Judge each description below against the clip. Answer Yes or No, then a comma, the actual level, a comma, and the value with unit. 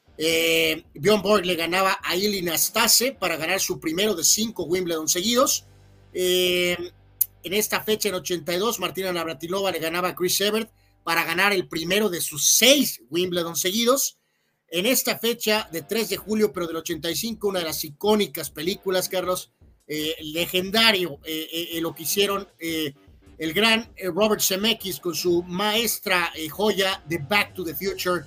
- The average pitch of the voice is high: No, medium, 180 Hz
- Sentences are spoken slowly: No, average, 160 wpm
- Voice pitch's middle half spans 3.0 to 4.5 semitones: Yes, average, 4.0 semitones